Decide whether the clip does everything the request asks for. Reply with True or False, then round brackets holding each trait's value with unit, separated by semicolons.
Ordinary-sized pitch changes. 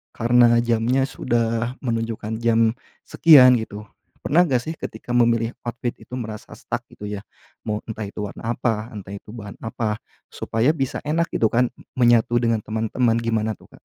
False (1.9 semitones)